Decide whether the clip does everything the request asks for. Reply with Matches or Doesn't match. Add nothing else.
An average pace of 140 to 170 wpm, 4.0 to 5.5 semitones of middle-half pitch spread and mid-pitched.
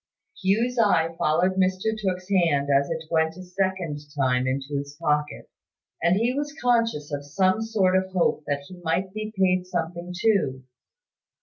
Matches